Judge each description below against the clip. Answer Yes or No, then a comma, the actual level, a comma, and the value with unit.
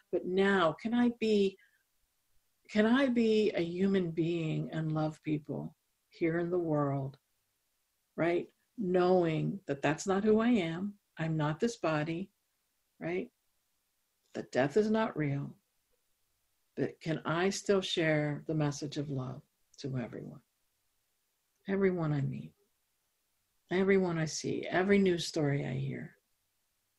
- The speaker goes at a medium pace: No, slow, 130 wpm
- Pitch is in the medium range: Yes, medium, 165 Hz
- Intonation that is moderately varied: Yes, average, 4.9 semitones